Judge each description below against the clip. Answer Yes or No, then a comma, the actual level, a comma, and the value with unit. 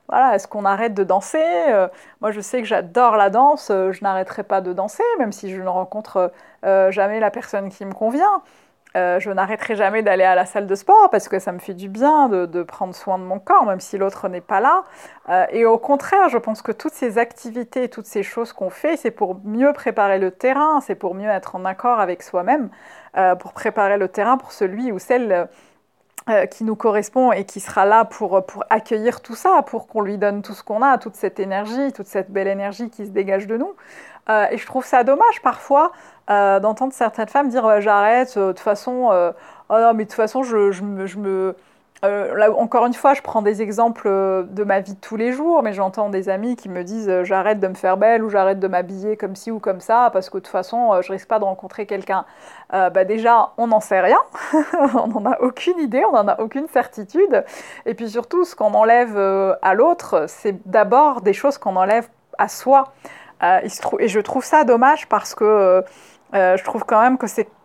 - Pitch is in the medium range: No, high, 215 Hz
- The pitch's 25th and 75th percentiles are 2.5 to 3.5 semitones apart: No, average, 4.0 semitones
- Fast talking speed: Yes, fast, 225 wpm